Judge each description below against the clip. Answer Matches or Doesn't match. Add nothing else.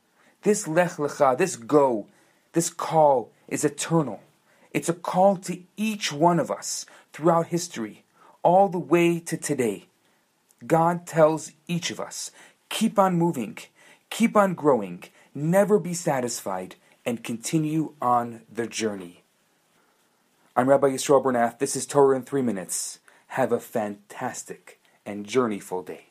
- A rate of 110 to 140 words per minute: Matches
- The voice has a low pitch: Doesn't match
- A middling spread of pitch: Doesn't match